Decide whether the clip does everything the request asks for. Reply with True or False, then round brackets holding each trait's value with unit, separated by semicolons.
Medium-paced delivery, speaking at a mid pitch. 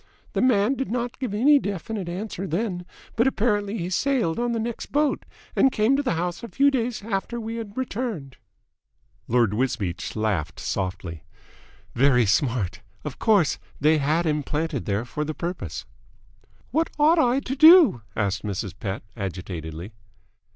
True (160 wpm; 180 Hz)